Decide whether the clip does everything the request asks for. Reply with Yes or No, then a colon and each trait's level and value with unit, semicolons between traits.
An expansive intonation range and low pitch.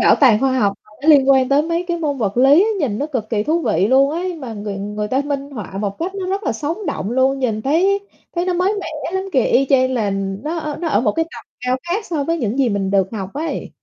No: wide, 6.9 semitones; very high, 275 Hz